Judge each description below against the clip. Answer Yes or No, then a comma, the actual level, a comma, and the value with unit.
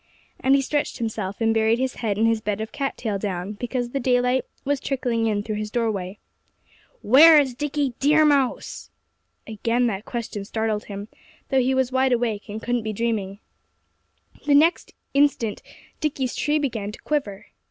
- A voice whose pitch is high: Yes, high, 235 Hz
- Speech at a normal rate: Yes, average, 170 wpm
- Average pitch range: Yes, average, 3.9 semitones